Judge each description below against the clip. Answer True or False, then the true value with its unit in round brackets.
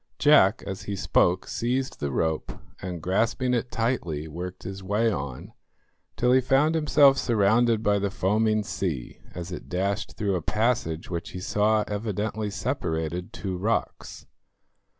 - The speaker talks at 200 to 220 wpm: False (150 wpm)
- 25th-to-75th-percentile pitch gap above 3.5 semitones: True (4.3 semitones)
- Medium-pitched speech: False (100 Hz)